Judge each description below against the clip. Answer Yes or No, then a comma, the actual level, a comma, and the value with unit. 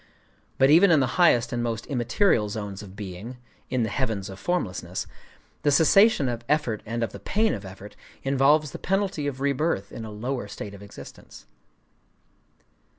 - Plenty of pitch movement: Yes, wide, 5.9 semitones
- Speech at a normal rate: Yes, average, 160 wpm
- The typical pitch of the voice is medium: No, low, 120 Hz